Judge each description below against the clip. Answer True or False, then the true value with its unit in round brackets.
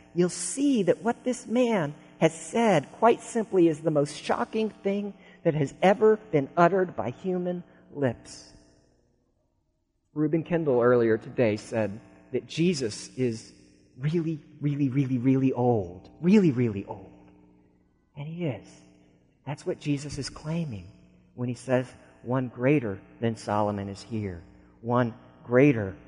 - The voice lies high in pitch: False (135 Hz)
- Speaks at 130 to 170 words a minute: True (135 wpm)